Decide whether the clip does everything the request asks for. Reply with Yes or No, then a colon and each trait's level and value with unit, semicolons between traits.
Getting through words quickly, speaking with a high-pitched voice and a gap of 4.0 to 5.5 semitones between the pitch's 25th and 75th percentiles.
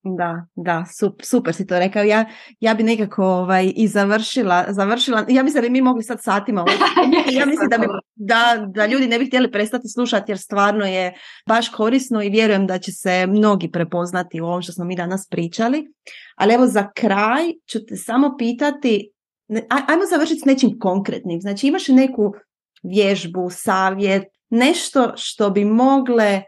Yes: fast, 175 wpm; high, 215 Hz; average, 4.4 semitones